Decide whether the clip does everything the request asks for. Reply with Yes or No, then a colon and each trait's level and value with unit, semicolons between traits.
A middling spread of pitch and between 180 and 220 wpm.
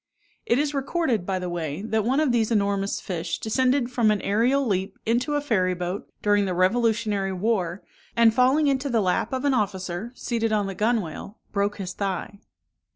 Yes: average, 4.2 semitones; average, 185 wpm